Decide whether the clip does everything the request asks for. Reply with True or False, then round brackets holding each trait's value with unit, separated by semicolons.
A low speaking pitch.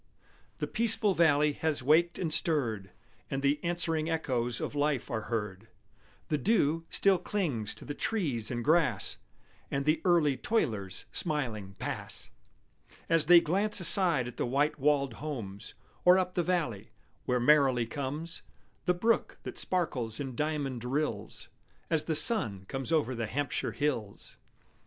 False (145 Hz)